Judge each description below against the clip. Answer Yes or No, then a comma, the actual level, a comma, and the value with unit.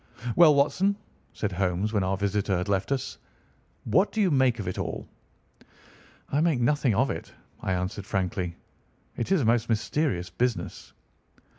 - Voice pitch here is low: Yes, low, 110 Hz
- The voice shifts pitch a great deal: Yes, wide, 6.7 semitones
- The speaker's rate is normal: Yes, average, 160 wpm